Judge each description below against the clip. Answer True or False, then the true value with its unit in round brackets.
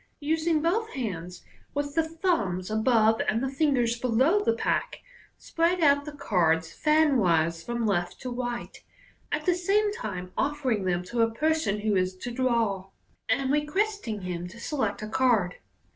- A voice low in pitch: False (240 Hz)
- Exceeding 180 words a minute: False (160 wpm)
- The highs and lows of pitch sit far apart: True (7.4 semitones)